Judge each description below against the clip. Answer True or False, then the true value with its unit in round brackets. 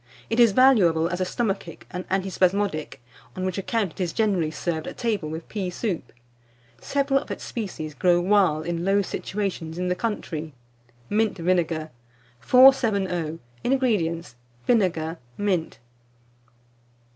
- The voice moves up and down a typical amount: True (4.1 semitones)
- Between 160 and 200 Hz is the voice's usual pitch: True (185 Hz)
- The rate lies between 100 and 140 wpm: True (135 wpm)